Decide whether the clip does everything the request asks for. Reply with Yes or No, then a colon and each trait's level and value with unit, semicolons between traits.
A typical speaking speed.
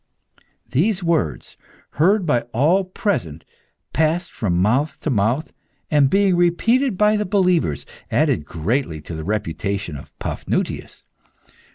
No: slow, 125 wpm